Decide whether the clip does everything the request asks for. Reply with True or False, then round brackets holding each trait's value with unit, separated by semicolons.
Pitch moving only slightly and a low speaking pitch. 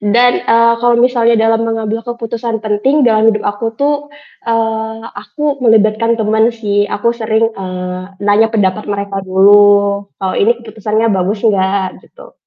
False (2.2 semitones; 220 Hz)